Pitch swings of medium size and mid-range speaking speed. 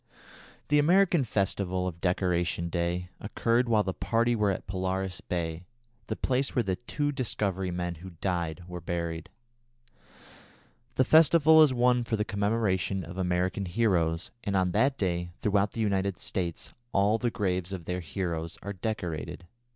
Yes: average, 4.3 semitones; average, 155 wpm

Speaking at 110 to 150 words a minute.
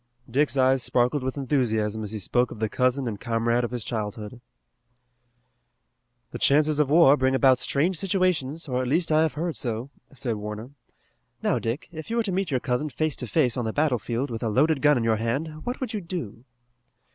No: fast, 205 wpm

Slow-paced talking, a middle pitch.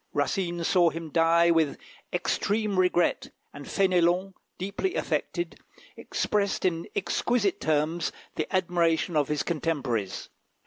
Yes: slow, 115 wpm; medium, 170 Hz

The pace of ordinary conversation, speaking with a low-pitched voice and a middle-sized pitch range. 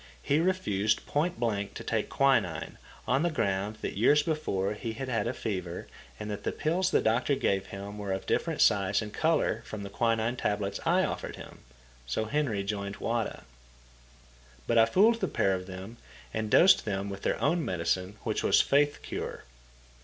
No: average, 180 wpm; low, 110 Hz; wide, 5.8 semitones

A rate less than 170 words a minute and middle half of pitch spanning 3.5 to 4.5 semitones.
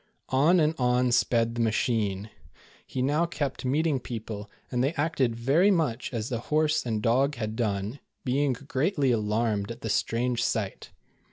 Yes: average, 160 wpm; average, 4.1 semitones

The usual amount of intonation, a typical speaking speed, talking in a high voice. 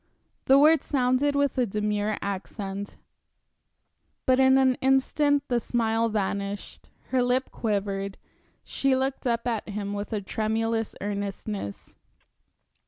No: average, 4.4 semitones; slow, 120 wpm; high, 225 Hz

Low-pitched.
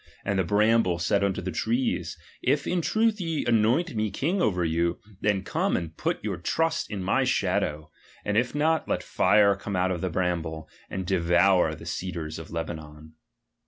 Yes: very low, 95 Hz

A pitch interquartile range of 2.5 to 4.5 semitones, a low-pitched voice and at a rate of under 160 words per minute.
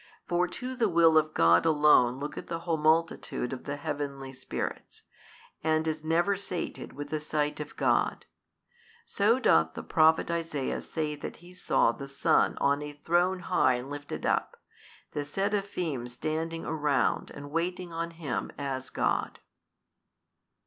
No: average, 3.0 semitones; medium, 155 Hz; average, 150 wpm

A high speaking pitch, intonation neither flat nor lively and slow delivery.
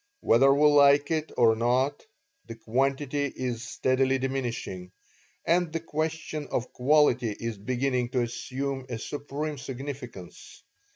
No: low, 135 Hz; average, 3.2 semitones; slow, 125 wpm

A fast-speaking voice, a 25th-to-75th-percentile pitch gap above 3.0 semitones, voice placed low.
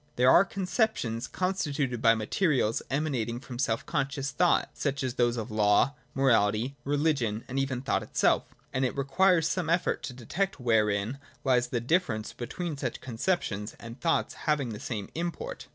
No: average, 175 wpm; average, 5.2 semitones; low, 130 Hz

